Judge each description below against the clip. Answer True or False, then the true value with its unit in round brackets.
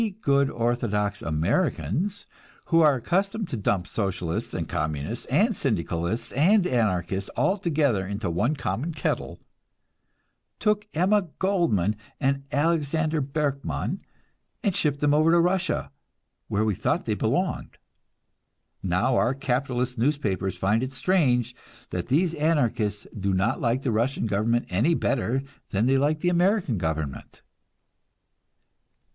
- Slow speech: True (130 wpm)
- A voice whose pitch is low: True (130 Hz)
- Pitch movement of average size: False (7.5 semitones)